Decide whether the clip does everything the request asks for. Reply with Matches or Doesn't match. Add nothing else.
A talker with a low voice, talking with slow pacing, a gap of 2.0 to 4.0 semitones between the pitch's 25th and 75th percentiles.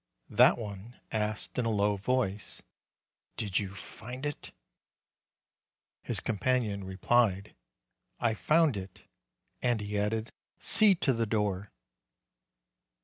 Matches